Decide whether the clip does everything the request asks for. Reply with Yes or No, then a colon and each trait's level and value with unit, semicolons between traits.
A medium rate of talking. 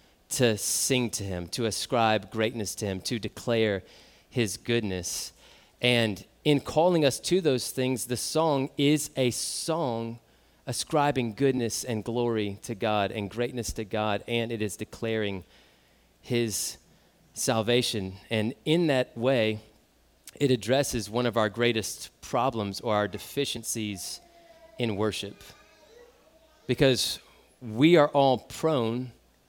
No: slow, 125 wpm